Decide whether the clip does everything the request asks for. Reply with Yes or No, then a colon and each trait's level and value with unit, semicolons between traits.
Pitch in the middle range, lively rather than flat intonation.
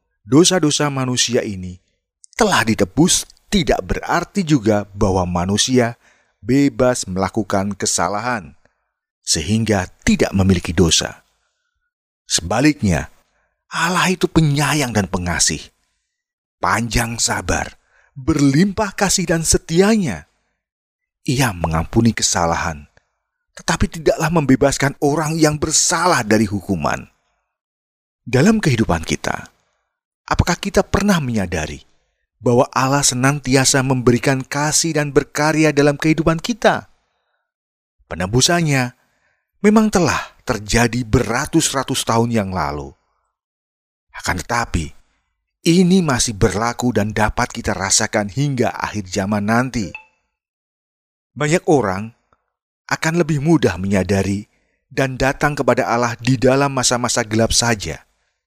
No: low, 125 Hz; wide, 6.9 semitones